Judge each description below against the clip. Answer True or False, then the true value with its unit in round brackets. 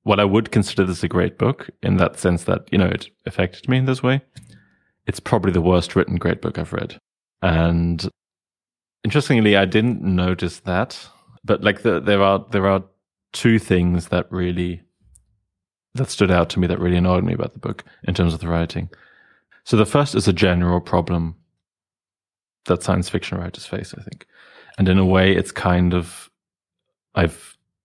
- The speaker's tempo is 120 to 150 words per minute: False (185 wpm)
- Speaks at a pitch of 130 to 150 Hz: False (95 Hz)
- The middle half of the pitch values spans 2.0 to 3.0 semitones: True (2.7 semitones)